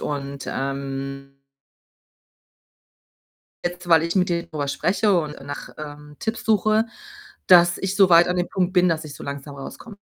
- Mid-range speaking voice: Yes, medium, 170 Hz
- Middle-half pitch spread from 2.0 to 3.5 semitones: No, average, 4.4 semitones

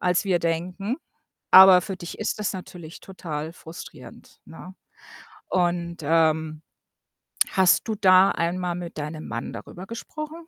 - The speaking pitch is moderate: Yes, medium, 180 Hz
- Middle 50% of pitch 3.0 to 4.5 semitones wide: No, narrow, 2.5 semitones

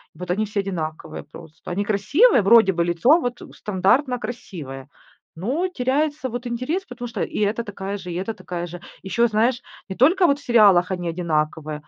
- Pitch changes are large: Yes, wide, 5.8 semitones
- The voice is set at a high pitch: Yes, high, 205 Hz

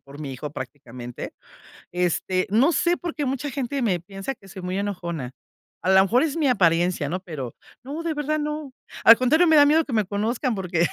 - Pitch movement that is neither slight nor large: No, wide, 8.7 semitones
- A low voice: No, high, 205 Hz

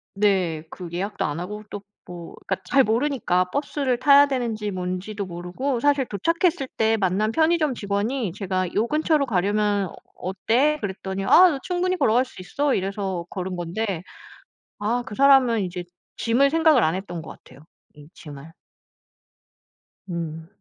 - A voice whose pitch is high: Yes, high, 210 Hz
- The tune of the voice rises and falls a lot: Yes, wide, 6.6 semitones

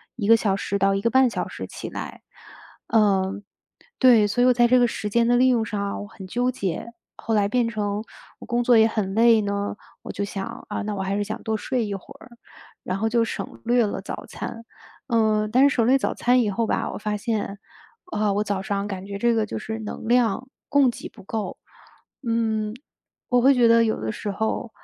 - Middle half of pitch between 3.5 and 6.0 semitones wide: No, average, 2.7 semitones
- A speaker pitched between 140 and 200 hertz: No, high, 220 Hz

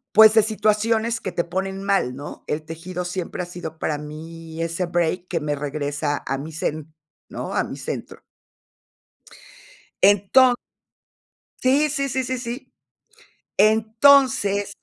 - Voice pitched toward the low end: No, medium, 185 Hz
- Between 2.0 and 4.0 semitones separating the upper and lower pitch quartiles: No, wide, 5.6 semitones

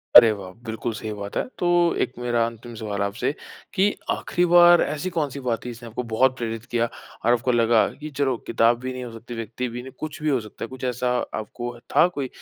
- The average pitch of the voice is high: No, low, 120 Hz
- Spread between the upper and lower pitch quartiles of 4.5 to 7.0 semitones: No, narrow, 2.5 semitones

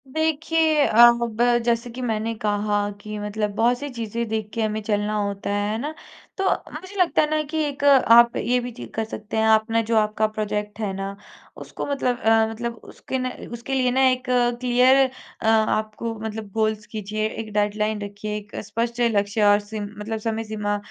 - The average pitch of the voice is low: No, high, 220 Hz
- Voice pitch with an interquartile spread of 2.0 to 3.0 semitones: Yes, average, 2.7 semitones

